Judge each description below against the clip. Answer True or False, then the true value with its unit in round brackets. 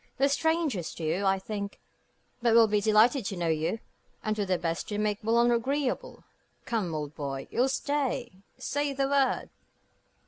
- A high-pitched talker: True (220 Hz)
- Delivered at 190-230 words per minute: False (170 wpm)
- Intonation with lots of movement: True (6.2 semitones)